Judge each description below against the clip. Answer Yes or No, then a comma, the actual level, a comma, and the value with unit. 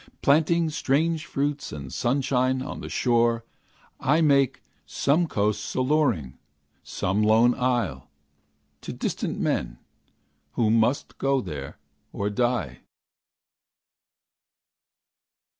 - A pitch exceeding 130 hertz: No, low, 125 Hz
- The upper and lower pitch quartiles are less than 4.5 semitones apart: No, average, 5.1 semitones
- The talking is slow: Yes, slow, 95 wpm